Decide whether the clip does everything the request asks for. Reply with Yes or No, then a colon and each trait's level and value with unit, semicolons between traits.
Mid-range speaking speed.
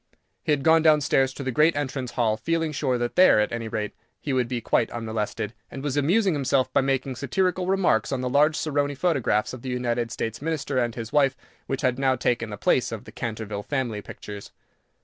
No: fast, 215 wpm